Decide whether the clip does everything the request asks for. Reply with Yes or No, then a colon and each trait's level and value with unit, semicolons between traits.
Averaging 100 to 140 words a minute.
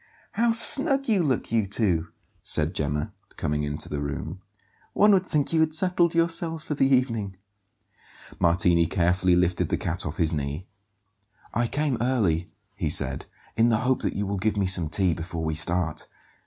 No: average, 175 wpm